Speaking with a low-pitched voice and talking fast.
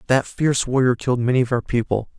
Yes: low, 125 Hz; fast, 220 wpm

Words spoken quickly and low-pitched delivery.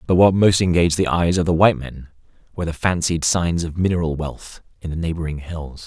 Yes: fast, 215 wpm; very low, 85 Hz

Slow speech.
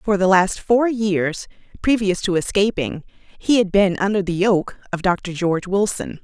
No: average, 175 wpm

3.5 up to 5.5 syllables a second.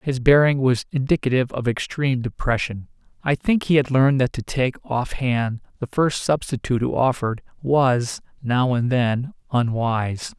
Yes: 4.9 syllables/s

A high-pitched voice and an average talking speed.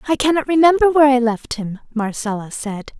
Yes: very high, 260 Hz; average, 180 wpm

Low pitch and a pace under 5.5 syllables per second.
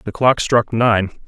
Yes: low, 115 Hz; 3.7 syllables/s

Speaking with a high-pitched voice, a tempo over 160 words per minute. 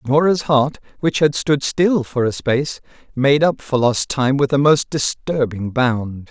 No: low, 135 Hz; average, 180 wpm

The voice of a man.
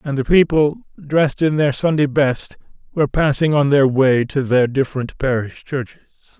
Yes: male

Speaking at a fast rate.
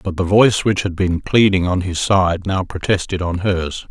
Yes: fast, 215 wpm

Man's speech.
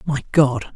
Yes: male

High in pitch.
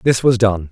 No: low, 110 Hz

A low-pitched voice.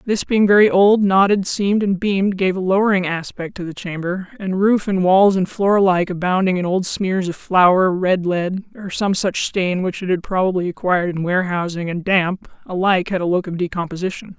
No: medium, 185 Hz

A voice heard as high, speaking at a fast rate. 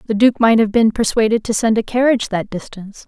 Yes: high, 220 Hz; fast, 235 wpm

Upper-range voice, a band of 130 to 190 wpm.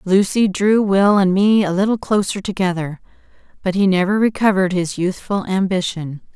Yes: high, 195 Hz; average, 150 wpm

